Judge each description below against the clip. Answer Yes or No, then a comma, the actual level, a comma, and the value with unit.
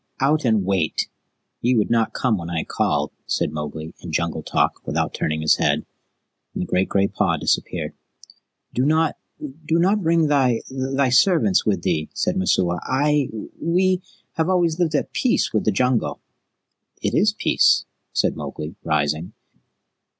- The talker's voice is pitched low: Yes, low, 125 Hz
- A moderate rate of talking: Yes, average, 160 wpm